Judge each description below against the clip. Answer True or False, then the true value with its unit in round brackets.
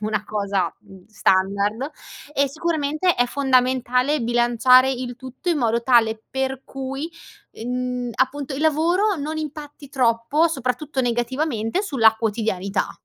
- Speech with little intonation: False (3.8 semitones)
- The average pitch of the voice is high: True (255 Hz)